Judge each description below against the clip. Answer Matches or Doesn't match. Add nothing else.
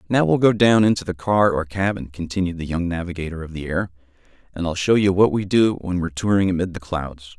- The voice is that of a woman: Doesn't match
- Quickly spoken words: Matches